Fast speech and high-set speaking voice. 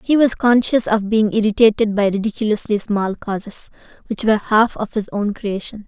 No: average, 175 wpm; high, 215 Hz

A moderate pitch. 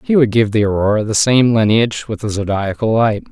No: low, 110 Hz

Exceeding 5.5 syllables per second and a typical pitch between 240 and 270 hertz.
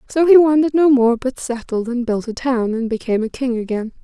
Yes: 5.8 syllables/s; very high, 250 Hz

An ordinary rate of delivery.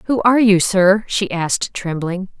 Yes: average, 175 wpm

